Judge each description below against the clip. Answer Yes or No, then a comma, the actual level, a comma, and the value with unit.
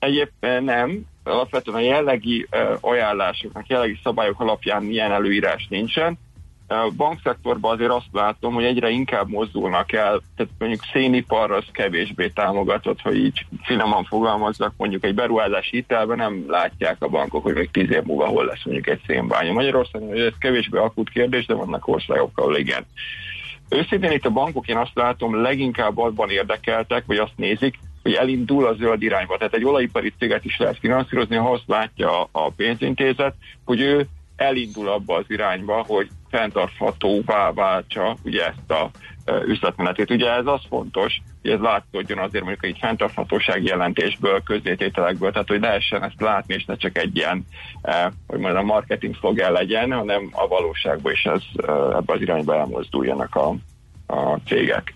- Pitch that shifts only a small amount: No, average, 3.2 semitones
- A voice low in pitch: Yes, low, 120 Hz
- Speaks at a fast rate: Yes, fast, 160 wpm